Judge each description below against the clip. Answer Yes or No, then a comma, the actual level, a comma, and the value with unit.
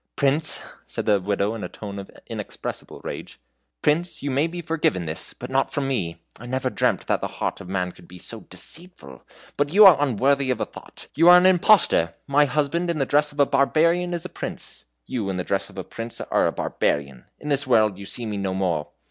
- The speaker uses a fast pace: Yes, fast, 225 wpm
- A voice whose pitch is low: Yes, low, 130 Hz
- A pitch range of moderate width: No, wide, 7.7 semitones